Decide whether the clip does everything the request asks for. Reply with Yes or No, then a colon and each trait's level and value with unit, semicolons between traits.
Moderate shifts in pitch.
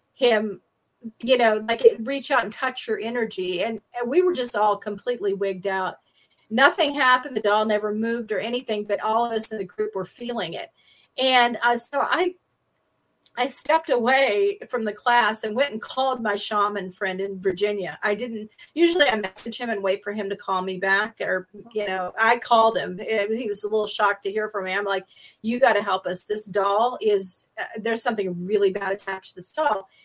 Yes: average, 3.3 semitones